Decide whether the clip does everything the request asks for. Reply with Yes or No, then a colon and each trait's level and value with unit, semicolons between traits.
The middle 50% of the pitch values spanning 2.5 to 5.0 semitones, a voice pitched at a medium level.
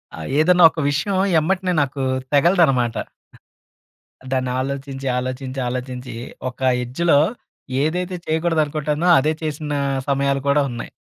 Yes: average, 3.5 semitones; medium, 145 Hz